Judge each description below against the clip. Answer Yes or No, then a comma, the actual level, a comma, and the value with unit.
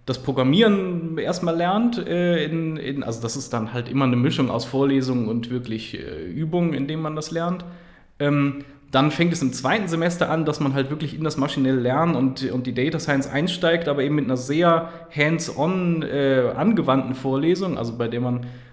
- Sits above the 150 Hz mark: No, medium, 145 Hz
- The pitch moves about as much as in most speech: Yes, average, 4.1 semitones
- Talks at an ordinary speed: No, fast, 195 wpm